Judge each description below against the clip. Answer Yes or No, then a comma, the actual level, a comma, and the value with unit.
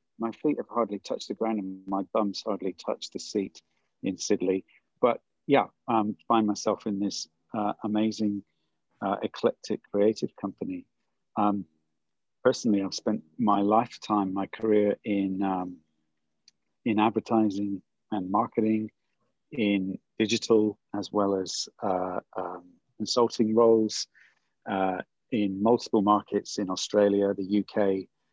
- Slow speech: Yes, slow, 130 wpm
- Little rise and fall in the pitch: Yes, narrow, 2.3 semitones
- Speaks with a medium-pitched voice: No, low, 105 Hz